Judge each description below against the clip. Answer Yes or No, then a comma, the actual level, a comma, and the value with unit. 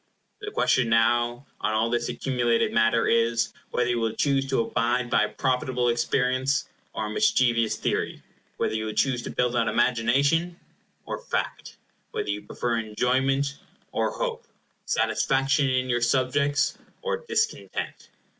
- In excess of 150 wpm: No, average, 145 wpm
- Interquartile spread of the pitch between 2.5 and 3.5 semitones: Yes, average, 2.8 semitones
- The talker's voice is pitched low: Yes, low, 125 Hz